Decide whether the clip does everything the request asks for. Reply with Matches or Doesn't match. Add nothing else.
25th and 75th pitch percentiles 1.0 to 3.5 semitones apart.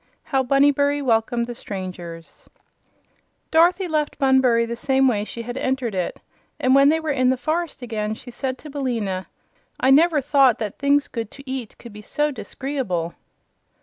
Doesn't match